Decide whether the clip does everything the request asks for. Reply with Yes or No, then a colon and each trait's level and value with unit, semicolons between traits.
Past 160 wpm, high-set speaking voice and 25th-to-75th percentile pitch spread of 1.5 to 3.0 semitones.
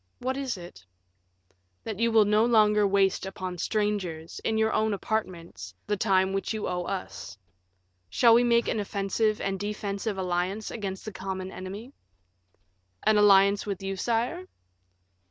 No: average, 150 wpm; high, 200 Hz; narrow, 2.5 semitones